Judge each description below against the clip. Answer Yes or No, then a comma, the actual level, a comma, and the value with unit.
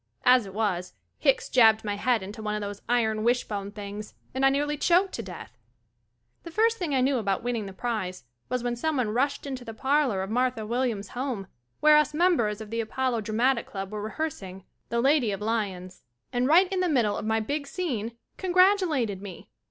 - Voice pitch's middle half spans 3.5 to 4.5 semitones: No, average, 4.9 semitones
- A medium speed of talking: No, fast, 220 wpm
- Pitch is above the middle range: Yes, high, 235 Hz